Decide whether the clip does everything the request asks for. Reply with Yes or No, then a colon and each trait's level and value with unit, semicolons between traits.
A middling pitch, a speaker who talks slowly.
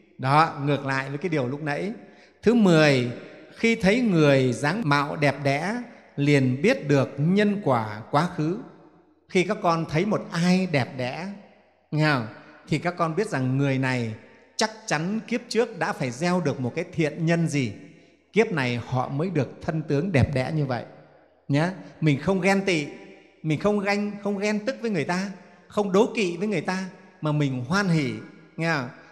No: medium, 160 Hz; average, 185 wpm